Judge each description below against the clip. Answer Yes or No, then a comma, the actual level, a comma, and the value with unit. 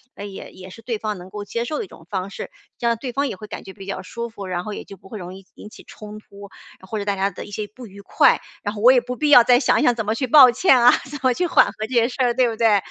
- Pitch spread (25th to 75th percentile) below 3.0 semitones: No, average, 3.5 semitones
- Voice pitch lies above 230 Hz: No, high, 215 Hz